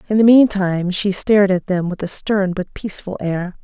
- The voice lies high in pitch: Yes, high, 195 Hz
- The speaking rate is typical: No, fast, 215 wpm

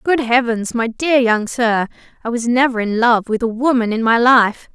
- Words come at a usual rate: No, fast, 215 wpm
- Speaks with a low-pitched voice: No, high, 235 Hz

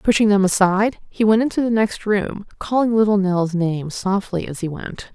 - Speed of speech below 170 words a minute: No, average, 200 wpm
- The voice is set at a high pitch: Yes, high, 200 Hz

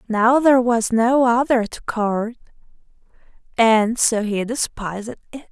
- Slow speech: Yes, slow, 130 wpm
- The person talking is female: Yes, female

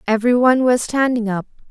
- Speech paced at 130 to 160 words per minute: Yes, average, 140 wpm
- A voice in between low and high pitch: No, high, 235 Hz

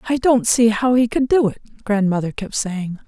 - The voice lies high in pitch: Yes, high, 225 Hz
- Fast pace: Yes, fast, 215 wpm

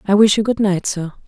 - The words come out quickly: Yes, fast, 280 wpm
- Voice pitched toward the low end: No, high, 200 Hz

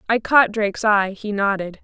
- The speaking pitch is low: No, high, 210 Hz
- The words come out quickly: No, average, 195 wpm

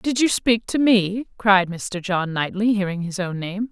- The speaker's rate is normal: No, fast, 210 wpm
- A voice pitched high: Yes, high, 200 Hz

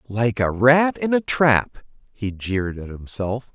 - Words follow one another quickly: No, average, 170 wpm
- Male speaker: Yes, male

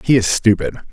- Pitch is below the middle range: Yes, low, 100 Hz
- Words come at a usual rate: Yes, average, 195 wpm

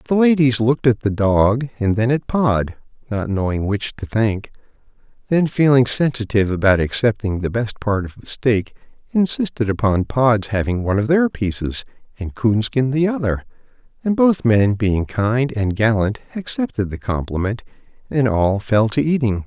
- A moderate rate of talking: Yes, average, 165 wpm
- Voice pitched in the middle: No, low, 115 Hz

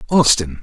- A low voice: Yes, low, 115 Hz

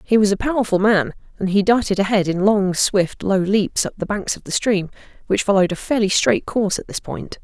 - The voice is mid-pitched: No, high, 200 Hz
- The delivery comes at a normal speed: No, fast, 235 wpm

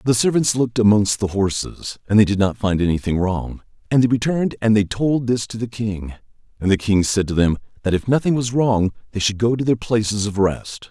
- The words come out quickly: Yes, fast, 230 wpm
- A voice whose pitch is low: Yes, low, 110 Hz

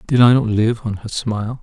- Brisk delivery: Yes, fast, 260 wpm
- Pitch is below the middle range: Yes, low, 115 Hz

